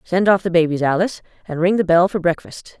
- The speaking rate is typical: No, fast, 235 wpm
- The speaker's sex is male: No, female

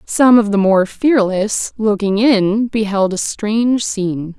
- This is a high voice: Yes, high, 210 Hz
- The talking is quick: No, average, 150 wpm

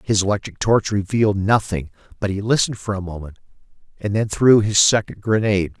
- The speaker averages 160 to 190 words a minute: Yes, average, 175 wpm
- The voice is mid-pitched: No, low, 105 Hz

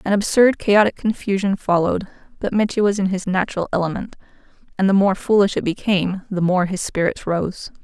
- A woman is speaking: Yes, female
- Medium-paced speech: Yes, average, 175 wpm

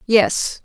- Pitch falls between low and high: No, high, 220 Hz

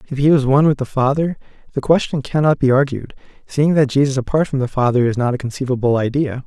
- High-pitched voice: No, low, 135 Hz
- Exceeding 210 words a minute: Yes, fast, 225 wpm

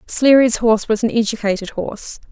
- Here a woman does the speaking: Yes, female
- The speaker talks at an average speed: Yes, average, 155 wpm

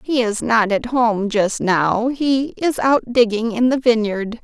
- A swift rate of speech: No, average, 190 wpm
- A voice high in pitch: Yes, high, 230 Hz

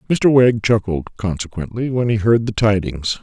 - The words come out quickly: No, average, 165 wpm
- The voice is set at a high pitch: No, low, 105 Hz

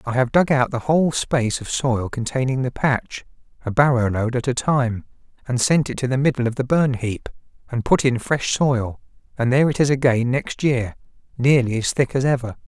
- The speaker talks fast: Yes, fast, 210 wpm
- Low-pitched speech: Yes, low, 130 Hz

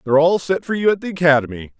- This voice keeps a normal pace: No, fast, 265 wpm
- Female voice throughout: No, male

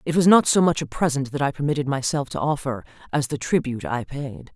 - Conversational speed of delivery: No, fast, 235 wpm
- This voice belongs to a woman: Yes, female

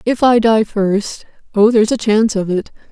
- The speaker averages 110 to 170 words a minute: No, fast, 205 wpm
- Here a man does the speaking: No, female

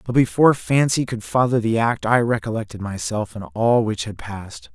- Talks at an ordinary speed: Yes, average, 190 wpm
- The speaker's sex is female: No, male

